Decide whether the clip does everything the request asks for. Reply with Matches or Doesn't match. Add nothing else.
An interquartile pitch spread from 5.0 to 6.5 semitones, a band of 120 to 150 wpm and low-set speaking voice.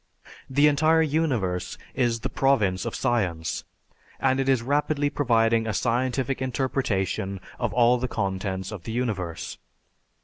Matches